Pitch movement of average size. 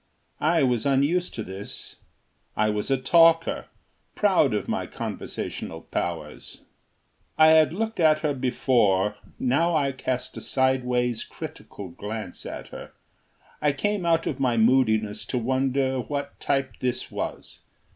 Yes: average, 4.6 semitones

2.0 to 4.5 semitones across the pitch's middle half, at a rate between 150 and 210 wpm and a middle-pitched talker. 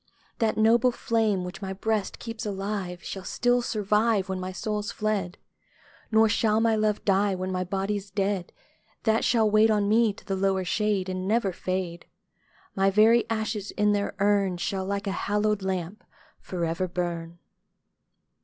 No: narrow, 2.4 semitones; average, 165 wpm; high, 200 Hz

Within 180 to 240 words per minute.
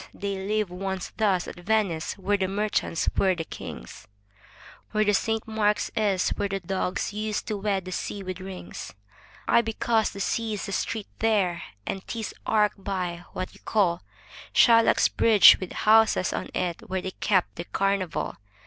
No: average, 170 wpm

